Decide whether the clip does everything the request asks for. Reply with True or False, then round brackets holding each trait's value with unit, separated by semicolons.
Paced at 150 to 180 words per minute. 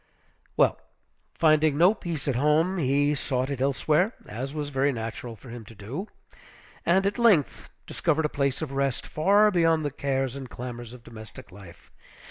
True (170 wpm)